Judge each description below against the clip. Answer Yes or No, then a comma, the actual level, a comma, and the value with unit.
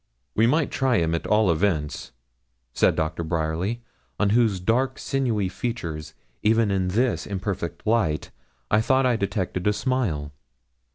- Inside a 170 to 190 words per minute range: No, average, 140 wpm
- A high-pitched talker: No, low, 100 Hz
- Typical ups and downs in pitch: No, wide, 5.7 semitones